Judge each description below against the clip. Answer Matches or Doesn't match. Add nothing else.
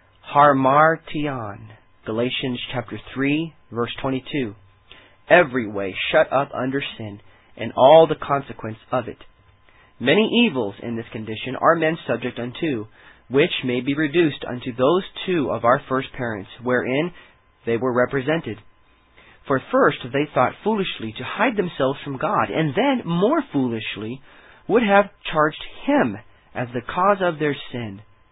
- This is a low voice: Matches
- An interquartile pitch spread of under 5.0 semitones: Doesn't match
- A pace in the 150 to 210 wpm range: Doesn't match